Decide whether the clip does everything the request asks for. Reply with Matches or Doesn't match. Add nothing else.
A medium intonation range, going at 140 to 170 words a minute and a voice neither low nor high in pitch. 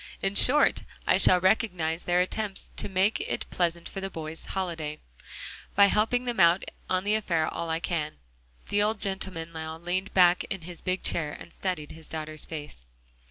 Doesn't match